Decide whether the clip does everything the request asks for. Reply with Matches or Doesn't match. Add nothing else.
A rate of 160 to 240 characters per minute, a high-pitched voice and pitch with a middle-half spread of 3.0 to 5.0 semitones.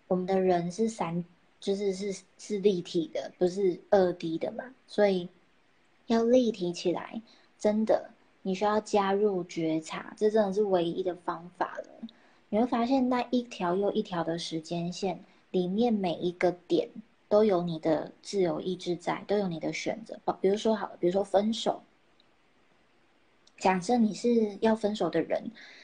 Matches